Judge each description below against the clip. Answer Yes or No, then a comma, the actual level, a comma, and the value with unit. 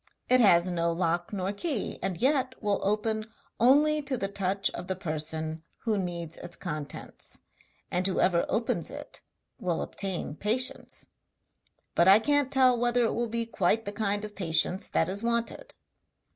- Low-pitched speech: No, high, 200 Hz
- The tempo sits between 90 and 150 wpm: No, average, 160 wpm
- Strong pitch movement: No, average, 4.9 semitones